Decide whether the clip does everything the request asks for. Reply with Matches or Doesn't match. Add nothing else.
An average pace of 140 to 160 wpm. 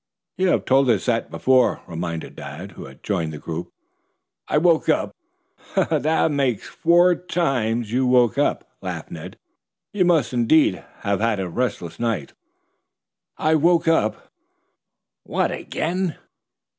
Matches